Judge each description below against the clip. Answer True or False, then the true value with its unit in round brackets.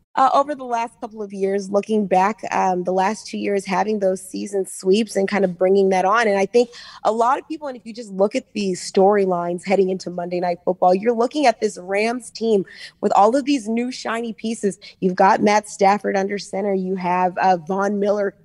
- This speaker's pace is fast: True (220 wpm)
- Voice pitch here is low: False (195 Hz)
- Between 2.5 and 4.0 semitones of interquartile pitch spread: True (2.8 semitones)